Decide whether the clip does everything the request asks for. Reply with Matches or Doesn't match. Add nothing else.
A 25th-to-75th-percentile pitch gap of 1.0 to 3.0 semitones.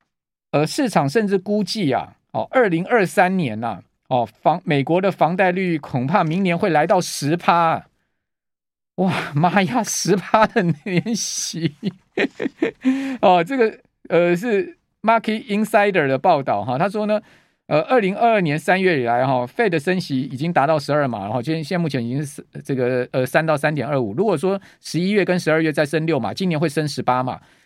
Doesn't match